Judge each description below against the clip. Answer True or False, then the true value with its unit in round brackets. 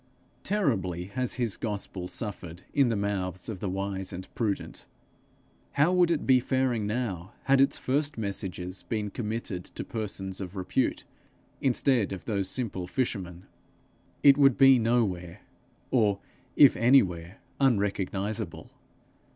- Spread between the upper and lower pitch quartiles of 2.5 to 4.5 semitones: False (5.1 semitones)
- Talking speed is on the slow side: True (130 wpm)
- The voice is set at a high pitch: False (105 Hz)